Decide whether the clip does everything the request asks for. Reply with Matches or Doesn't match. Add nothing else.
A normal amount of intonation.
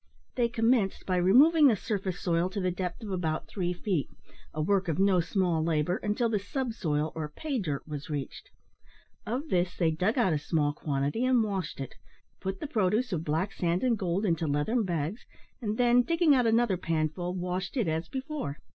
Doesn't match